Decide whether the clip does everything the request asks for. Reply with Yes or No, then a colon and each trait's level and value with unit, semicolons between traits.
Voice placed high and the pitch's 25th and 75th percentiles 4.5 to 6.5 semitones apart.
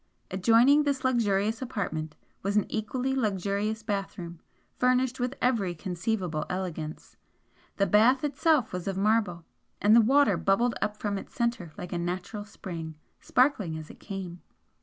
Yes: high, 205 Hz; average, 5.0 semitones